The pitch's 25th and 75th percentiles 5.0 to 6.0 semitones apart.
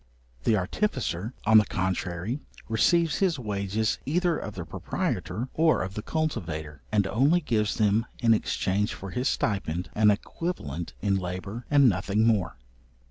Yes: wide, 5.4 semitones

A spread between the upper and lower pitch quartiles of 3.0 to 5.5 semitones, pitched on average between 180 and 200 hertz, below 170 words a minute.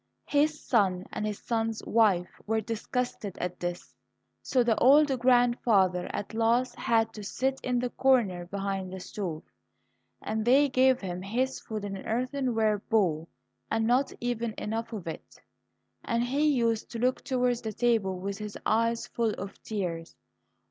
No: average, 3.8 semitones; high, 225 Hz; average, 160 wpm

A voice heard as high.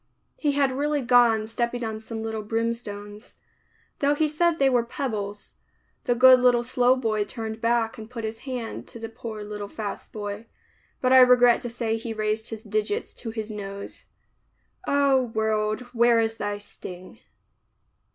Yes: high, 225 Hz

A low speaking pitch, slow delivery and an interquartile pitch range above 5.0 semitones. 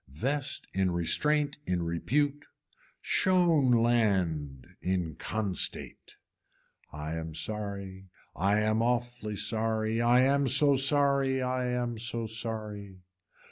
Yes: low, 110 Hz; slow, 105 wpm; wide, 5.6 semitones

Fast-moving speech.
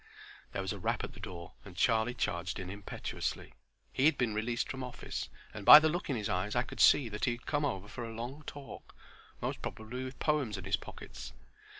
Yes: fast, 225 wpm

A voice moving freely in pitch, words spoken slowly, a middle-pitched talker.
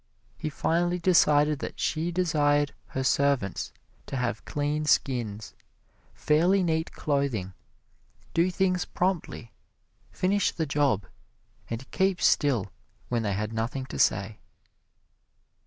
Yes: wide, 6.1 semitones; slow, 115 wpm; medium, 145 Hz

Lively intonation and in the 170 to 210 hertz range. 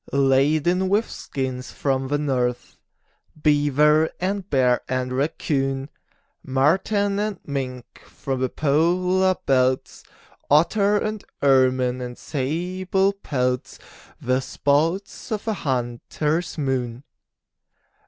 No: wide, 5.8 semitones; medium, 145 Hz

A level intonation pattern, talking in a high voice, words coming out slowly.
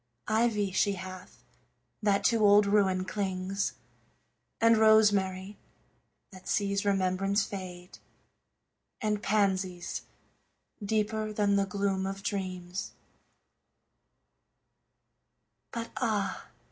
Yes: narrow, 1.9 semitones; high, 200 Hz; slow, 85 wpm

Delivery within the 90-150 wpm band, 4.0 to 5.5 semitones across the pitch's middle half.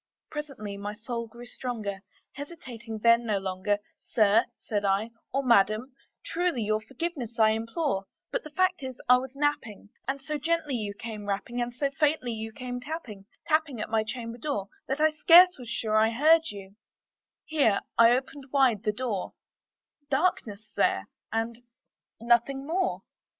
No: average, 160 wpm; average, 4.6 semitones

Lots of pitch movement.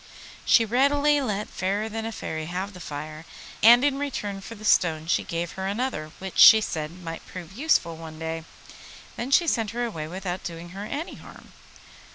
Yes: wide, 5.9 semitones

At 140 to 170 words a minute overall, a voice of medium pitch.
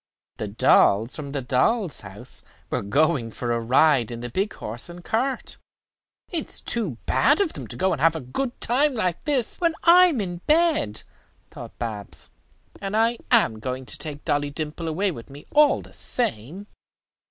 No: average, 185 wpm; medium, 160 Hz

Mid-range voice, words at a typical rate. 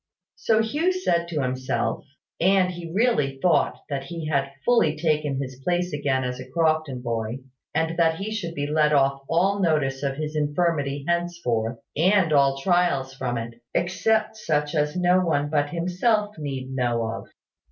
Yes: medium, 155 Hz; average, 165 wpm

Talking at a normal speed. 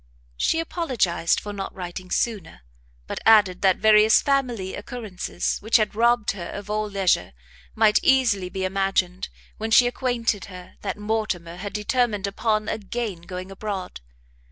Yes: average, 145 wpm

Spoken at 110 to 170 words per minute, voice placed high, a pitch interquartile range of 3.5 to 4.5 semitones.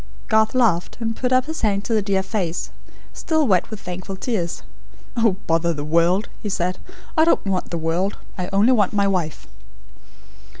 No: average, 180 wpm; high, 195 Hz; average, 4.1 semitones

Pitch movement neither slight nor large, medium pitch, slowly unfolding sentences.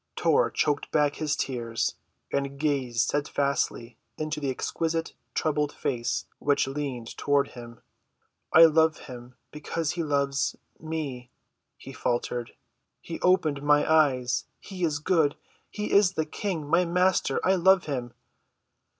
Yes: average, 3.3 semitones; medium, 145 Hz; slow, 125 wpm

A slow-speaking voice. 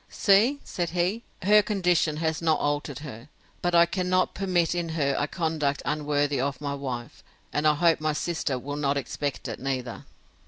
No: average, 180 wpm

